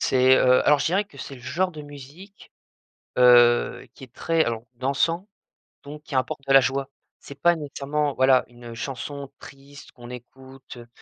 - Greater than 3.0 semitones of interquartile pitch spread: No, average, 2.7 semitones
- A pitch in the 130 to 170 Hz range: Yes, low, 135 Hz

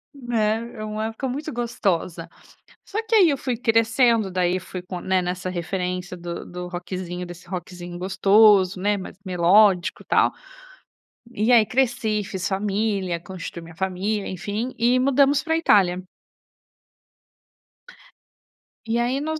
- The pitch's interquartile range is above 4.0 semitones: Yes, average, 4.4 semitones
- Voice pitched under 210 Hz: Yes, high, 200 Hz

